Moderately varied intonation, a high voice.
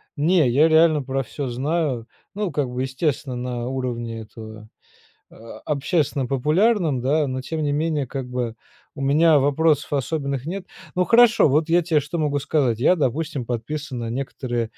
No: average, 4.1 semitones; medium, 140 Hz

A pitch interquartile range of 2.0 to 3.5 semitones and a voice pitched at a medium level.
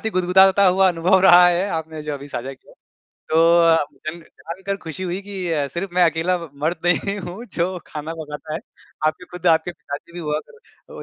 Yes: average, 2.8 semitones; medium, 170 Hz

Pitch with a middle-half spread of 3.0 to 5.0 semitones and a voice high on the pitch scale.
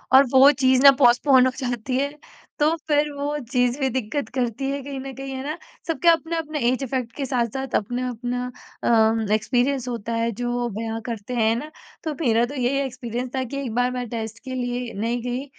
No: narrow, 2.6 semitones; very high, 250 Hz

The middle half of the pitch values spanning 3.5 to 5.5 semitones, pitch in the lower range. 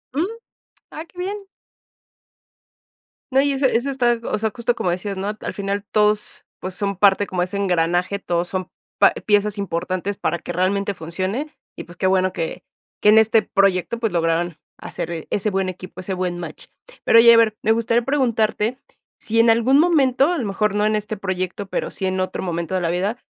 No: average, 3.8 semitones; high, 200 Hz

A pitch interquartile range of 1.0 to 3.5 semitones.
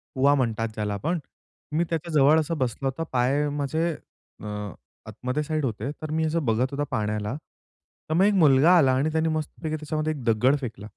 No: average, 4.3 semitones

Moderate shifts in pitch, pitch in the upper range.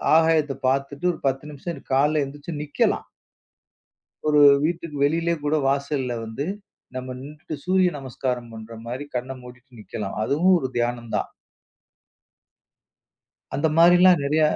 No: average, 3.9 semitones; medium, 145 Hz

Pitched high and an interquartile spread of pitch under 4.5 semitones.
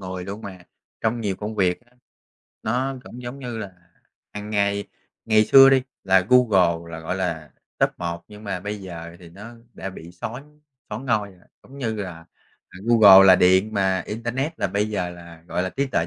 No: low, 100 Hz; average, 4.1 semitones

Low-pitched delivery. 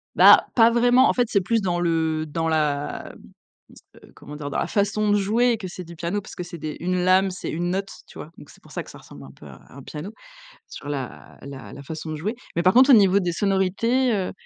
No: medium, 180 Hz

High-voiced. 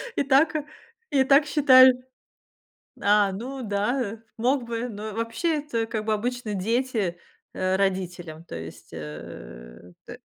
Yes: high, 220 Hz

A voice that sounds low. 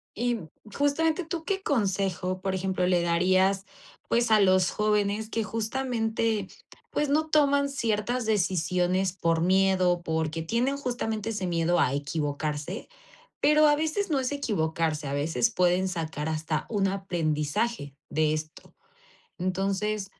No: high, 195 Hz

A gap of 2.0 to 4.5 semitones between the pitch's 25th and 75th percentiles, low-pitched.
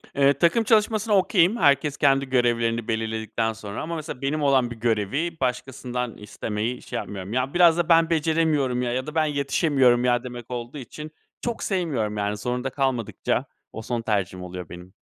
No: average, 5.2 semitones; low, 125 Hz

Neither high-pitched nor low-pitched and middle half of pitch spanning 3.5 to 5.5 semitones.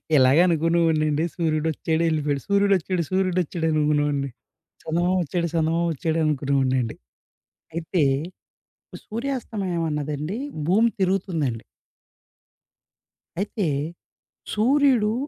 Yes: medium, 165 Hz; average, 3.9 semitones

